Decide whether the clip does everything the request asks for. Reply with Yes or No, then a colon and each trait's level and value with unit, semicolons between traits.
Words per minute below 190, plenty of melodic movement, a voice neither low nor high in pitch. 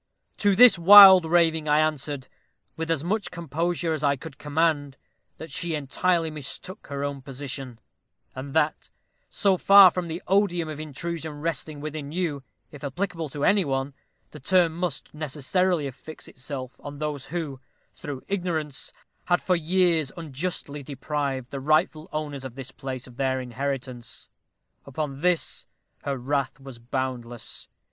No: average, 150 wpm; average, 3.8 semitones; medium, 150 Hz